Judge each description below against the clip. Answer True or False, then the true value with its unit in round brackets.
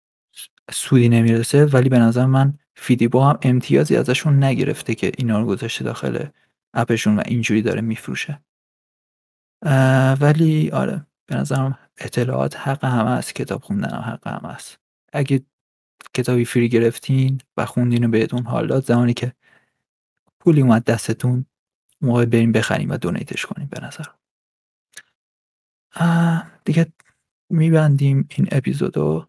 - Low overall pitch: True (125 Hz)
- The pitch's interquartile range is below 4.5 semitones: True (3.1 semitones)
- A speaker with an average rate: True (130 wpm)